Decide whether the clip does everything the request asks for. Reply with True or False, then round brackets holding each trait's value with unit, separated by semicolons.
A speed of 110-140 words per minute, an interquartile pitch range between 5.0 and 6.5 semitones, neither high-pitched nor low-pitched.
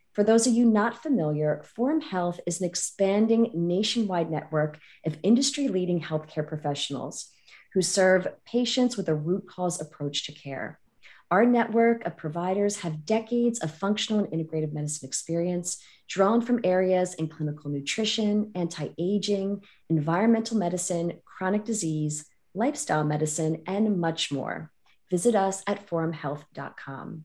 True (135 wpm; 5.3 semitones; 180 Hz)